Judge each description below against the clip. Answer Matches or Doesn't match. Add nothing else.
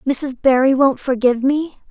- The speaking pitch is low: Doesn't match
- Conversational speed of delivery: Matches